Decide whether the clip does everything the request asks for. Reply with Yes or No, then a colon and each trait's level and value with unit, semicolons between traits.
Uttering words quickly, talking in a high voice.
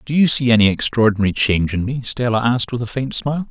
No: fast, 240 wpm; low, 120 Hz